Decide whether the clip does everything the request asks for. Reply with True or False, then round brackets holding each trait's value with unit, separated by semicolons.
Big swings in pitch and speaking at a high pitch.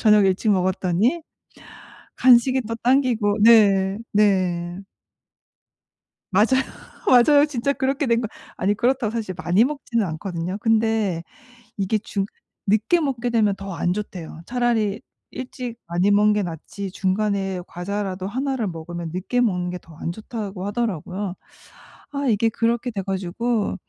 False (4.1 semitones; 210 Hz)